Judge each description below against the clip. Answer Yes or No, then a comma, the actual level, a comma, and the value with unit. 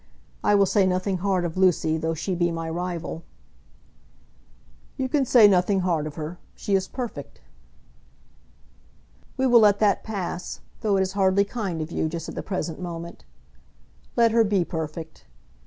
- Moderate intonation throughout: Yes, average, 3.4 semitones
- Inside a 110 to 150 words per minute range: No, average, 165 wpm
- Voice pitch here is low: No, medium, 185 Hz